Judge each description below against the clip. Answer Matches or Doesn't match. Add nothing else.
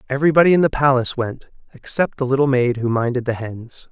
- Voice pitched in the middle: Doesn't match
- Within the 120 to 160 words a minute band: Doesn't match